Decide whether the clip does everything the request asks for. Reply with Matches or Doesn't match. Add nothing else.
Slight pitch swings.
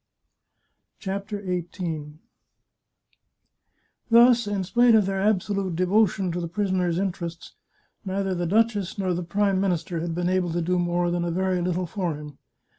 Matches